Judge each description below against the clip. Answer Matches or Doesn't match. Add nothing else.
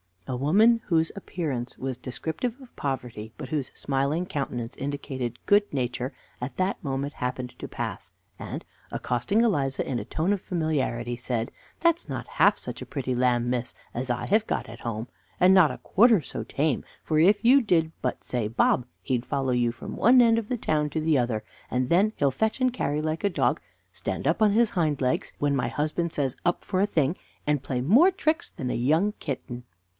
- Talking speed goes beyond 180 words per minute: Matches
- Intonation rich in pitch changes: Matches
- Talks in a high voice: Doesn't match